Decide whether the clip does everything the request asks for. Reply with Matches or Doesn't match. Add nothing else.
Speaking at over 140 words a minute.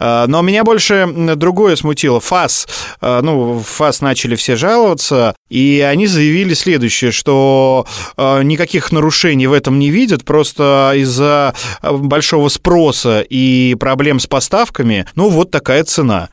Doesn't match